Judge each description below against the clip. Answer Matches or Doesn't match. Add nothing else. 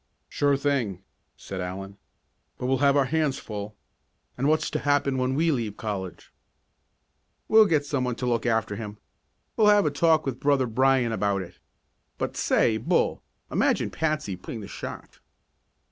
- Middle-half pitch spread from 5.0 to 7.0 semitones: Matches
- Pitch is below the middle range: Matches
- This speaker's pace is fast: Doesn't match